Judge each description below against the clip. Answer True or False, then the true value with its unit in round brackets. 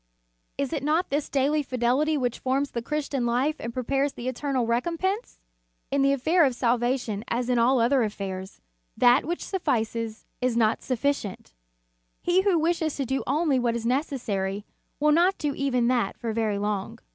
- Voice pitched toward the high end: True (260 Hz)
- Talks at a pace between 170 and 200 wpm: True (180 wpm)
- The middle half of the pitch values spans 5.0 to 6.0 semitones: False (4.0 semitones)